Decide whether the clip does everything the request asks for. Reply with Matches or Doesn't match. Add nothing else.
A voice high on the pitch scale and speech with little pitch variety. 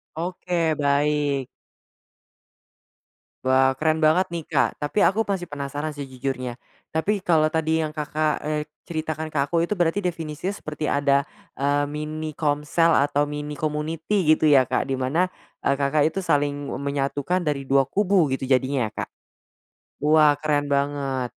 Doesn't match